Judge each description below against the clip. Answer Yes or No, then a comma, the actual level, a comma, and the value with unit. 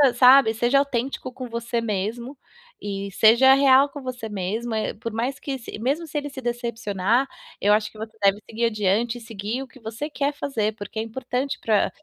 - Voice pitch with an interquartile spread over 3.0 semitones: Yes, average, 3.4 semitones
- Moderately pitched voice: No, high, 235 Hz